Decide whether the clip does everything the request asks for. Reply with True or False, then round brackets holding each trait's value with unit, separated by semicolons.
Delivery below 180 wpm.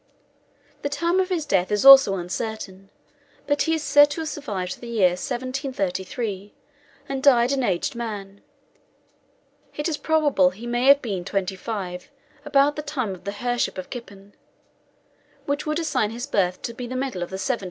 False (185 wpm)